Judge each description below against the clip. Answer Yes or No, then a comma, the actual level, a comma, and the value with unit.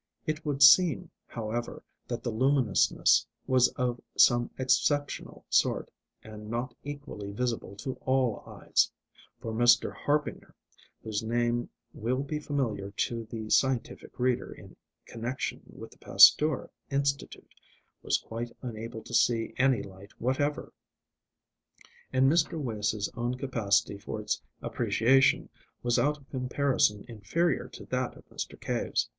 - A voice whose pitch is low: Yes, low, 125 Hz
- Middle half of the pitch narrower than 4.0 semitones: Yes, average, 3.4 semitones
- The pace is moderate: No, slow, 130 wpm